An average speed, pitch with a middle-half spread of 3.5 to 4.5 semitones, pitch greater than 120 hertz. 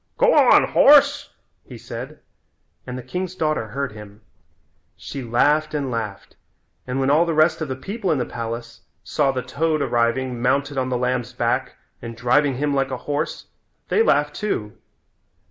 Yes: average, 170 wpm; average, 4.2 semitones; low, 135 Hz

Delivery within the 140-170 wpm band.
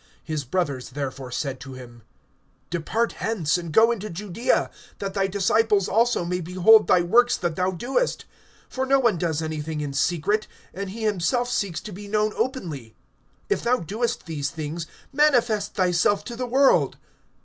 Yes: average, 165 wpm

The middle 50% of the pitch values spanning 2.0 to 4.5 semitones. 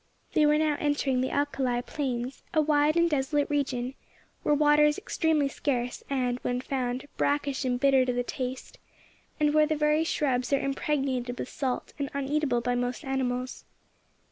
Yes: average, 2.9 semitones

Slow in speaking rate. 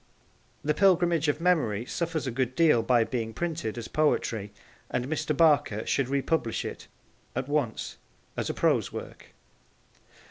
No: average, 145 wpm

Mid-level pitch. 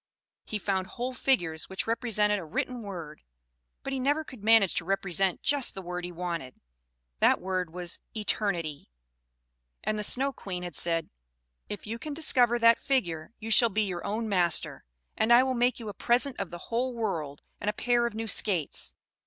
No: high, 210 Hz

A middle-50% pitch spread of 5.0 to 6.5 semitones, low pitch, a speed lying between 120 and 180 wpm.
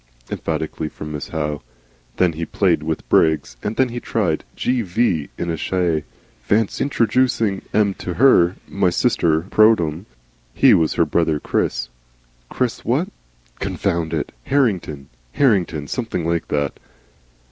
Yes: wide, 5.6 semitones; very low, 85 Hz; slow, 135 wpm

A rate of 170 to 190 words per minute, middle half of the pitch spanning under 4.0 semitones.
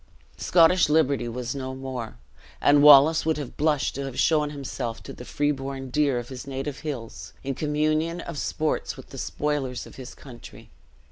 Yes: average, 180 wpm; narrow, 2.5 semitones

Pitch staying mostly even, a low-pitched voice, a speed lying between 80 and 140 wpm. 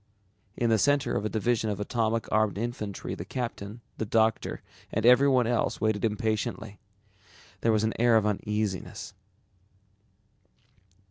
Yes: narrow, 2.0 semitones; low, 110 Hz; slow, 135 wpm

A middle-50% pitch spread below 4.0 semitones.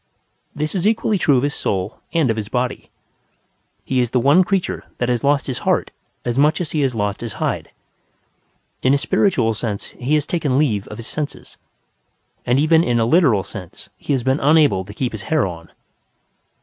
No: average, 5.1 semitones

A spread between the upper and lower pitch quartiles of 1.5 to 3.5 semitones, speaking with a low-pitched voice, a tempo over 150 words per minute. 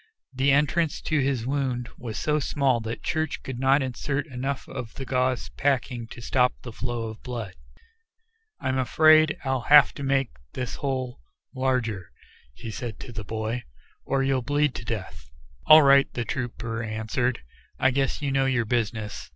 Yes: average, 2.8 semitones; low, 130 Hz; average, 165 wpm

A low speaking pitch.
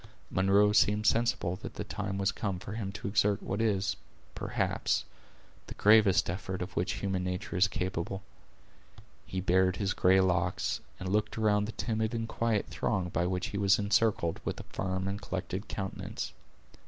Yes: low, 100 Hz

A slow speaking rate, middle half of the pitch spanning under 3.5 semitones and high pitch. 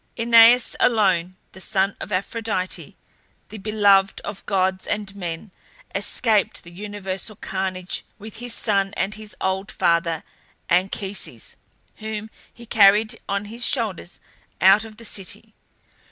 Yes: slow, 125 wpm; narrow, 2.5 semitones; high, 200 Hz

